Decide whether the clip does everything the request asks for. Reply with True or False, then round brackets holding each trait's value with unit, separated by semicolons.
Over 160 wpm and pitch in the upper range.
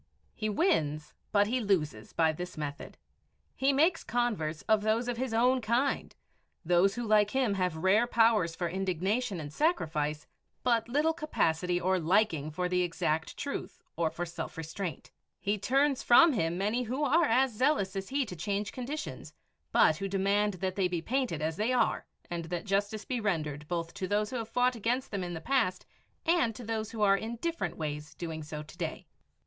True (190 wpm; 200 Hz)